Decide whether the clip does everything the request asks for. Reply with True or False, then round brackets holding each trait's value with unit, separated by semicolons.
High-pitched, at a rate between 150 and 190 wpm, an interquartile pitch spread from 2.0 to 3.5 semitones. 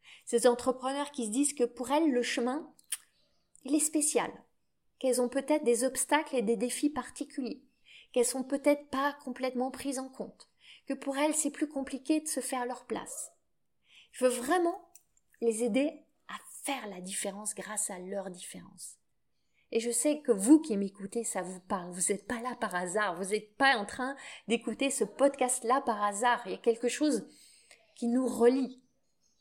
True (255 Hz; 180 wpm; 3.1 semitones)